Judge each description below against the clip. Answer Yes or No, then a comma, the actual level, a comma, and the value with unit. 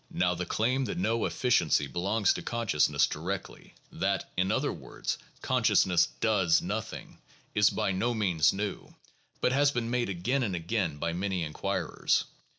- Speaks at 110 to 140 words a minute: No, average, 155 wpm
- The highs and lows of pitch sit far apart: No, average, 4.8 semitones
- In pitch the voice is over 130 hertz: No, low, 100 Hz